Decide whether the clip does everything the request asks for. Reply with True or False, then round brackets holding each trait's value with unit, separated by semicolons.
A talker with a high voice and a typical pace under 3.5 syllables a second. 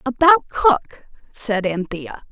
True (240 Hz; 3.2 syllables/s)